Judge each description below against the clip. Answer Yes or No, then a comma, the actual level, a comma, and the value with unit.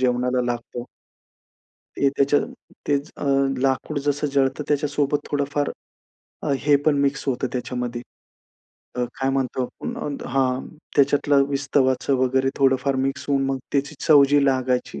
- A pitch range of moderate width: No, narrow, 1.7 semitones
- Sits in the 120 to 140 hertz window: Yes, low, 135 Hz